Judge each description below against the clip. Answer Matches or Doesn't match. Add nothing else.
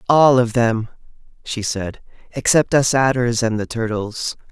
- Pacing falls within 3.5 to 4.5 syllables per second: Matches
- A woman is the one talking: Doesn't match